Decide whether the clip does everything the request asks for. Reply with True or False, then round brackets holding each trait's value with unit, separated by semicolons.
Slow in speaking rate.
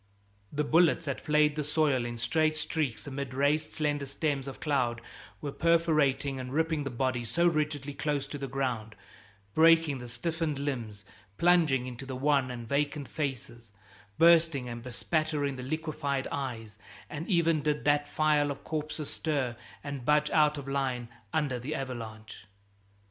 False (155 wpm)